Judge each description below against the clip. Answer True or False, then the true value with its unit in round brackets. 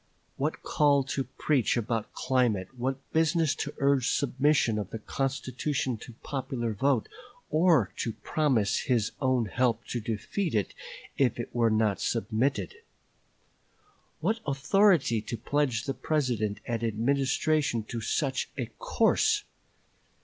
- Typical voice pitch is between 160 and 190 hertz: False (130 Hz)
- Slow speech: True (130 wpm)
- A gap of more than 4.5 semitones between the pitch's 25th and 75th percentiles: False (3.9 semitones)